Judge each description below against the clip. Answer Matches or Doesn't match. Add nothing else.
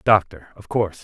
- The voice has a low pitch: Matches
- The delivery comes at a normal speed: Matches